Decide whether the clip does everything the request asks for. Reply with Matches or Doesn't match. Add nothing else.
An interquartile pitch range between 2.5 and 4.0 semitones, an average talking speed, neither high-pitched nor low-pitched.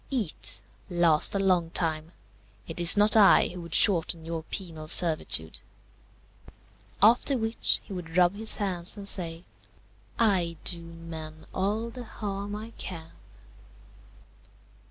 Doesn't match